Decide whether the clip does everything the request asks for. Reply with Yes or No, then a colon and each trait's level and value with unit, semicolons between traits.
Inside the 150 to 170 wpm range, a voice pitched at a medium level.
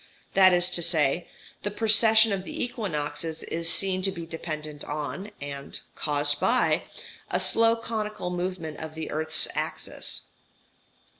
No: average, 140 wpm; medium, 175 Hz